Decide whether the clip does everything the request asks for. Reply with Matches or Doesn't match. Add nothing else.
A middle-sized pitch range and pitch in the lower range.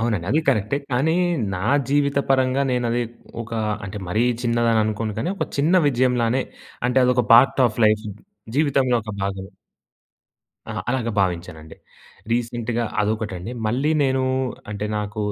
Matches